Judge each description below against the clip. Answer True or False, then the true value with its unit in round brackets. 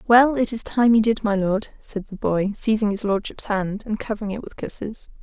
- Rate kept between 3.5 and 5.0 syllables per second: False (5.2 syllables/s)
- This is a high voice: True (210 Hz)